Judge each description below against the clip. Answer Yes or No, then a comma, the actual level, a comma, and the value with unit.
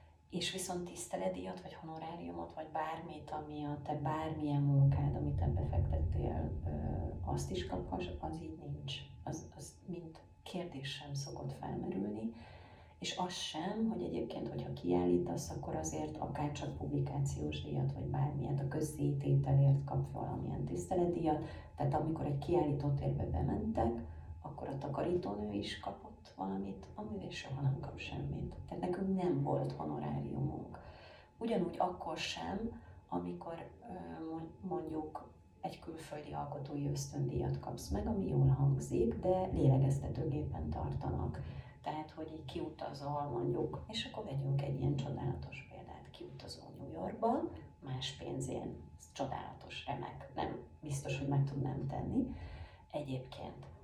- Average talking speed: Yes, average, 125 wpm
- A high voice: No, low, 130 Hz